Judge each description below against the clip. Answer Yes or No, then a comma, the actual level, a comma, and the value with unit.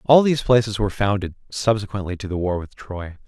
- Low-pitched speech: Yes, low, 105 Hz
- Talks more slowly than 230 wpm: Yes, average, 200 wpm